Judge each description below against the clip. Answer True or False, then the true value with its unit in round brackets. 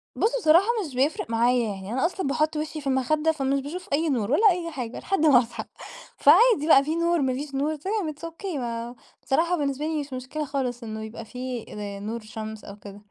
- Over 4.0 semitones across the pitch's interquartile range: True (4.9 semitones)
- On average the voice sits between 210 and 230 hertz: False (275 Hz)